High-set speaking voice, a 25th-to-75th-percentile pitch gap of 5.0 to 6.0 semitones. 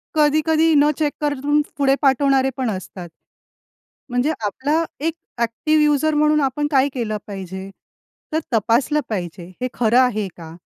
Yes: very high, 270 Hz; wide, 5.6 semitones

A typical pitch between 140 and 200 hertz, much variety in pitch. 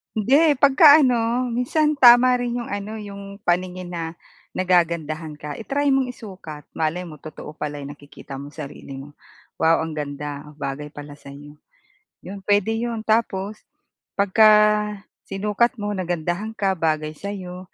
Yes: medium, 185 Hz; wide, 6.5 semitones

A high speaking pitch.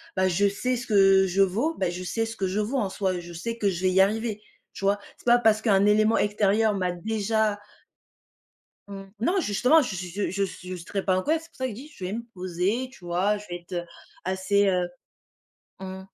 Yes: high, 200 Hz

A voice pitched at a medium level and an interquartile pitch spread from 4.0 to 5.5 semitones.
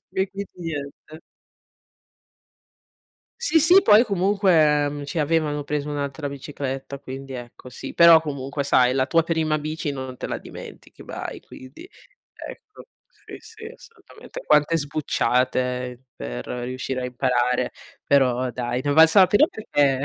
Yes: medium, 145 Hz; average, 4.3 semitones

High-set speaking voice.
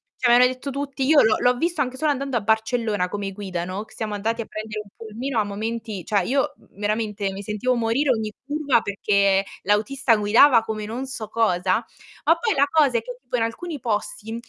Yes: high, 225 Hz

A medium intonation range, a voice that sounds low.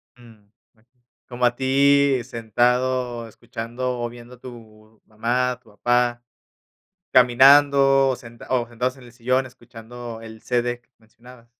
No: narrow, 1.5 semitones; low, 120 Hz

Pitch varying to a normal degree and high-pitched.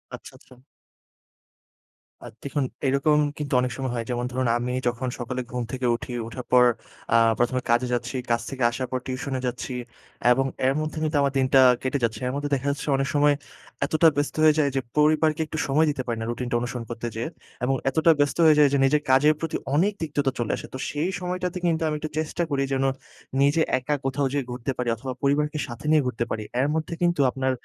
No: average, 3.2 semitones; low, 135 Hz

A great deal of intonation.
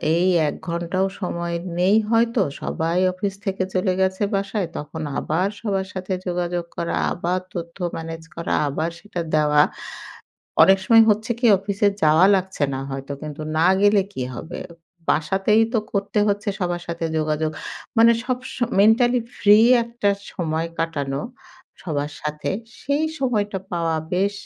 No: average, 3.9 semitones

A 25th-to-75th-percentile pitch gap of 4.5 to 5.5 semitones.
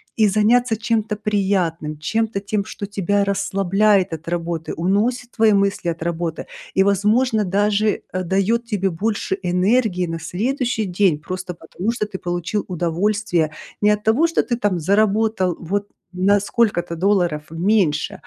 No: average, 3.4 semitones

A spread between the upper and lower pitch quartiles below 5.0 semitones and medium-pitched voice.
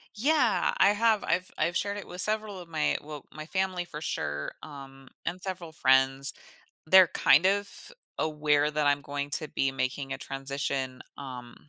No: wide, 5.5 semitones; medium, 155 Hz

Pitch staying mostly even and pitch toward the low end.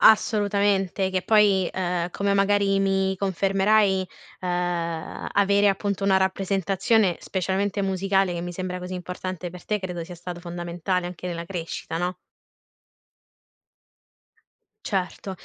No: narrow, 1.8 semitones; high, 190 Hz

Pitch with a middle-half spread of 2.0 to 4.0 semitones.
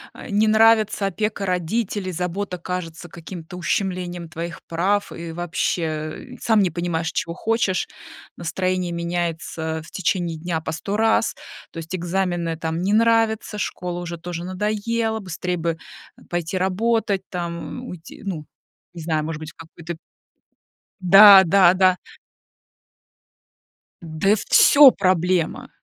Yes: average, 3.1 semitones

